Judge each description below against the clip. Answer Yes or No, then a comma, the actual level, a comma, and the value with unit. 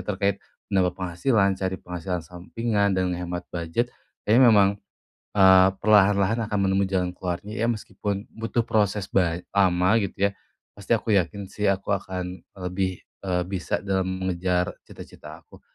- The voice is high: No, very low, 95 Hz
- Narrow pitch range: Yes, narrow, 2.2 semitones